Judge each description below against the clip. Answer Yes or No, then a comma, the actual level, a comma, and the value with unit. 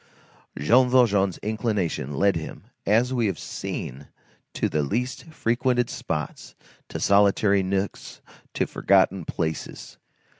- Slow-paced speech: Yes, slow, 115 wpm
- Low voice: Yes, low, 100 Hz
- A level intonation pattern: No, average, 5.1 semitones